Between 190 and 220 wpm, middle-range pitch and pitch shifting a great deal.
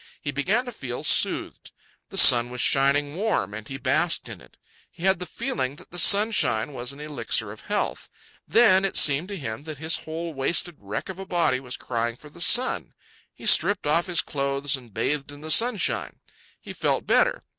Yes: average, 200 wpm; medium, 145 Hz; wide, 5.7 semitones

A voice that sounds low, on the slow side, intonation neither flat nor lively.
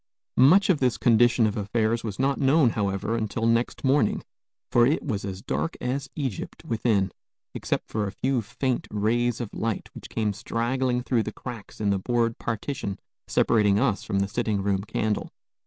No: low, 115 Hz; average, 175 wpm; average, 3.3 semitones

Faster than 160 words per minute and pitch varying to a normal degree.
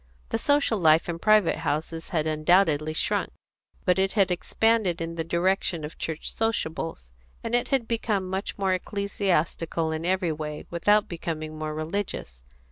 No: average, 155 wpm; average, 4.1 semitones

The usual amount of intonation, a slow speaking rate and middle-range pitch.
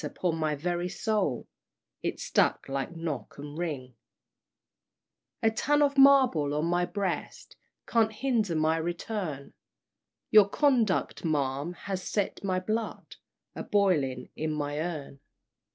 No: wide, 6.1 semitones; slow, 125 wpm; medium, 175 Hz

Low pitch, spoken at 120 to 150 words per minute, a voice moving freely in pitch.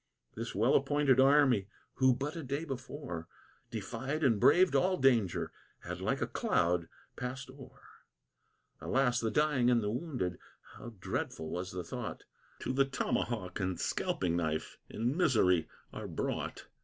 Yes: low, 125 Hz; average, 145 wpm; wide, 6.8 semitones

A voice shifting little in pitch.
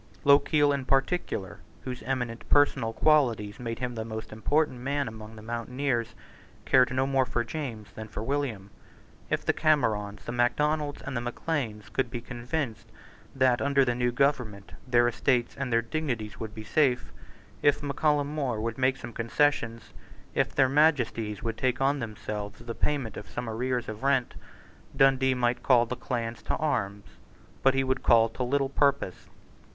No: average, 3.5 semitones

